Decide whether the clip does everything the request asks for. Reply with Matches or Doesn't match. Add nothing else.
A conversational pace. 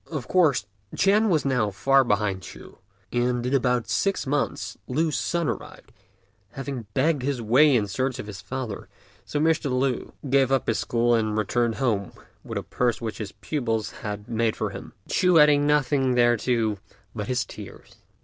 Matches